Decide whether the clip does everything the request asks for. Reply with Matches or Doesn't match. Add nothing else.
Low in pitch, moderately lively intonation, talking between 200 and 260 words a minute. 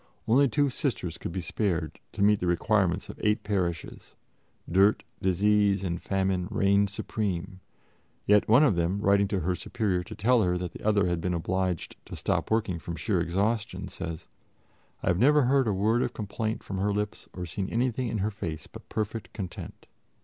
Doesn't match